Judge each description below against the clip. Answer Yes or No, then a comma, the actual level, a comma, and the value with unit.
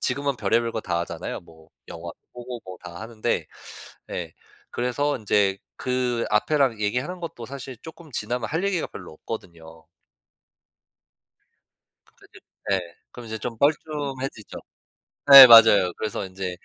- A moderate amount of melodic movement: No, wide, 5.8 semitones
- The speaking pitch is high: No, low, 115 Hz